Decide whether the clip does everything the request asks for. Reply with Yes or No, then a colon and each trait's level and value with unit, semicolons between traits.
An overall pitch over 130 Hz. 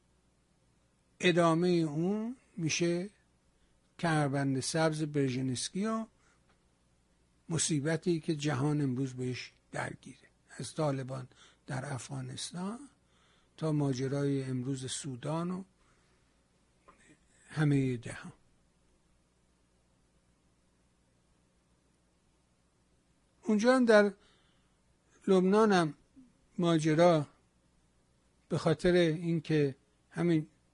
Yes: medium, 140 Hz